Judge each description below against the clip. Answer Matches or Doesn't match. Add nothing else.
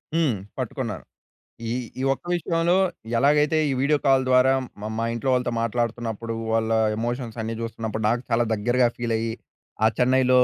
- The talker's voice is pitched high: Doesn't match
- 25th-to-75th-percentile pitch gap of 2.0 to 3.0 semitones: Matches